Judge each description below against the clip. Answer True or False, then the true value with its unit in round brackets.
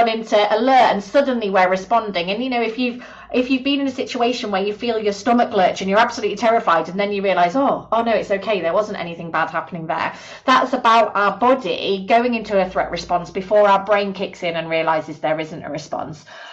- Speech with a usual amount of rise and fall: True (4.0 semitones)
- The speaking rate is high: True (225 wpm)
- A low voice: False (205 Hz)